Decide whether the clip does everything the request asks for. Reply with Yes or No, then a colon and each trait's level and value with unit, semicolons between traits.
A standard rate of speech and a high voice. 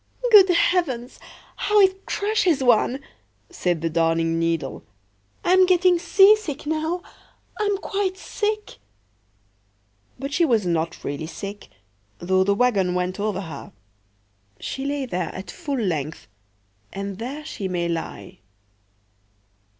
No: slow, 115 wpm; high, 210 Hz